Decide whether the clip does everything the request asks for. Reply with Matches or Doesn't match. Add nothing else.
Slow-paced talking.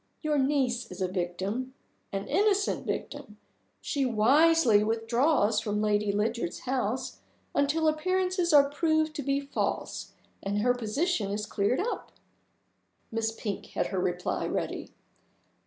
Matches